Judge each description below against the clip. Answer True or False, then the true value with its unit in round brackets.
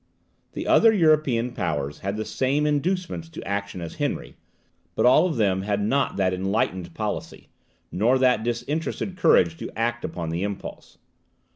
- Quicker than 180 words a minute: False (155 wpm)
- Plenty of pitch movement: True (7.4 semitones)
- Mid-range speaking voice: False (115 Hz)